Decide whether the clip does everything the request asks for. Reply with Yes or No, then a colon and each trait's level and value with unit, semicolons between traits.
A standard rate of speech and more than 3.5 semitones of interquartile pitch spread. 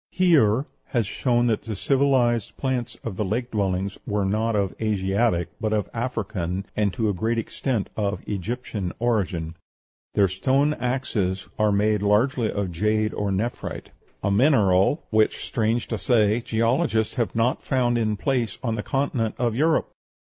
No: average, 155 wpm; average, 3.2 semitones